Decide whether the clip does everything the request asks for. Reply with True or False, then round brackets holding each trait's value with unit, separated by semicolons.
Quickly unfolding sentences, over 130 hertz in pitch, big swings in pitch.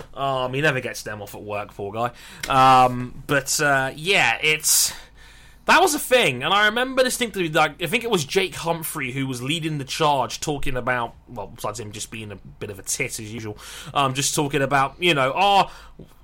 False (210 wpm; 140 Hz; 4.7 semitones)